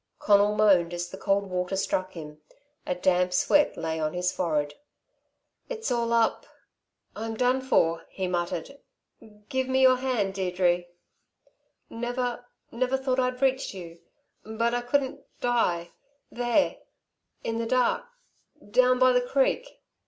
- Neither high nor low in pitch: No, high, 225 Hz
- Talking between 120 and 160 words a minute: Yes, average, 140 wpm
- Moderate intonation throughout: No, wide, 6.0 semitones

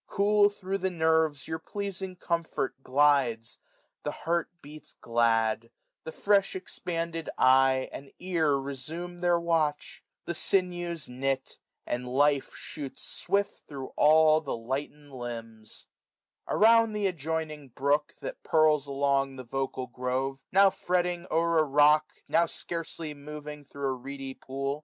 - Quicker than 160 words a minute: No, slow, 135 wpm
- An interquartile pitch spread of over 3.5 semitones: Yes, average, 4.1 semitones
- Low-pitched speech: No, medium, 150 Hz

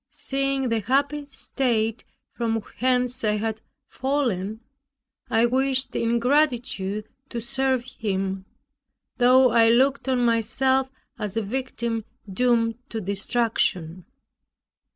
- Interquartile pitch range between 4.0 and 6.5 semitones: No, average, 3.1 semitones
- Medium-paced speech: No, slow, 110 wpm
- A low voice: No, high, 235 Hz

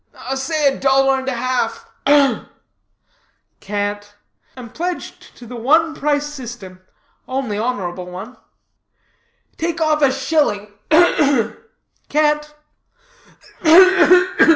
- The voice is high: Yes, very high, 265 Hz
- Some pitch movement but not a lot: Yes, average, 5.0 semitones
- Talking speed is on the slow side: Yes, slow, 100 wpm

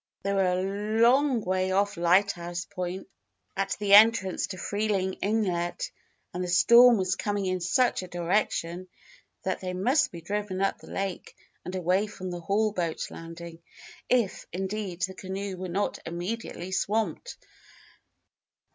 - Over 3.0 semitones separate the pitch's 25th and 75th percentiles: No, narrow, 2.4 semitones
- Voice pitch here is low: No, high, 190 Hz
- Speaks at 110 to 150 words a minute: Yes, average, 145 wpm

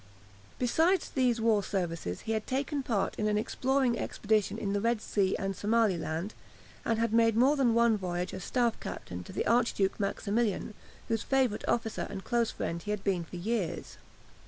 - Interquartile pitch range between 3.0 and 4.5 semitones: Yes, average, 3.3 semitones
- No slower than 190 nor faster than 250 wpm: No, average, 180 wpm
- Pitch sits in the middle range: No, high, 220 Hz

